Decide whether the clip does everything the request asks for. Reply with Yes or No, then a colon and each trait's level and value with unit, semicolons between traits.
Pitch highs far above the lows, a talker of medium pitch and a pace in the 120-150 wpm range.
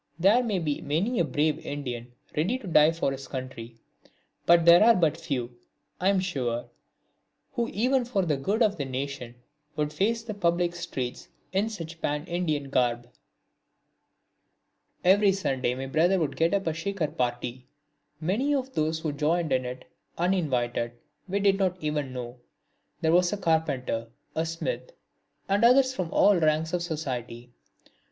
No: wide, 6.3 semitones; medium, 160 Hz; average, 160 wpm